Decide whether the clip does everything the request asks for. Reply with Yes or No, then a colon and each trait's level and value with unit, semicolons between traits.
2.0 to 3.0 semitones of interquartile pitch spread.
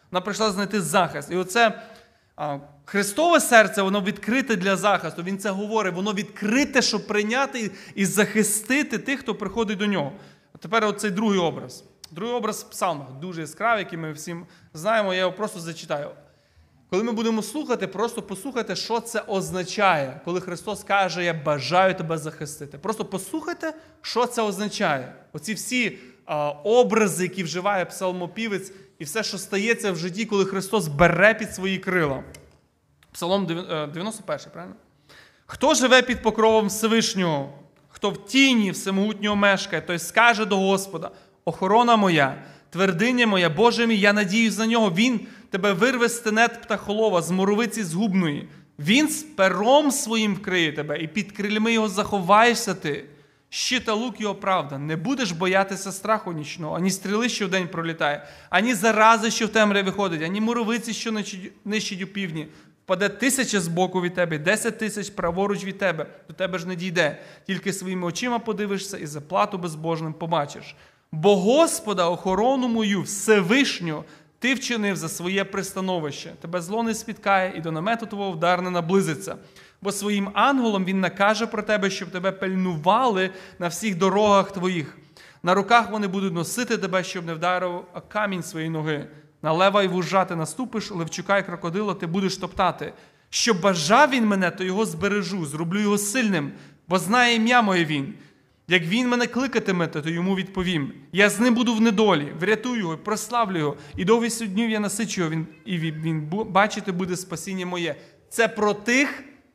No: average, 3.8 semitones